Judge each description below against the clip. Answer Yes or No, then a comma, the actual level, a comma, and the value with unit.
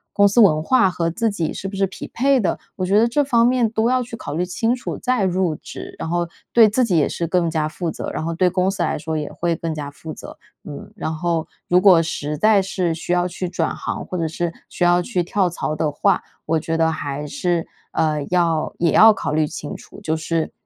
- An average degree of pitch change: Yes, average, 4.0 semitones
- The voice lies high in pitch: No, medium, 175 Hz